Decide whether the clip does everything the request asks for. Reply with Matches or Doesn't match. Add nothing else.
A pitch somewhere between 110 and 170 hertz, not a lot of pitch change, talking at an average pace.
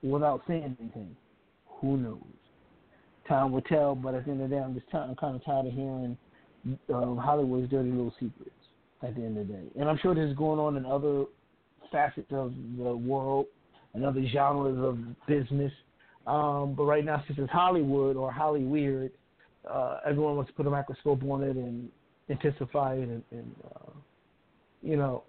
Matches